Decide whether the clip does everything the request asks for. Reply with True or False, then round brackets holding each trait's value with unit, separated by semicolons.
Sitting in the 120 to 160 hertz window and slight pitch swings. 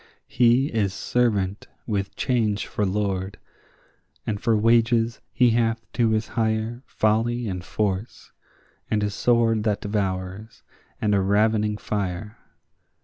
False (110 Hz; 2.3 semitones)